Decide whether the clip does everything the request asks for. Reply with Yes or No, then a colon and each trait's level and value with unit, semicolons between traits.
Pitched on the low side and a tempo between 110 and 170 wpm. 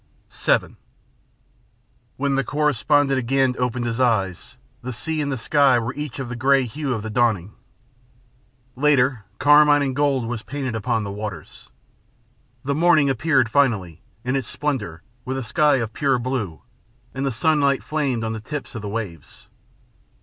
Yes: low, 130 Hz; average, 160 wpm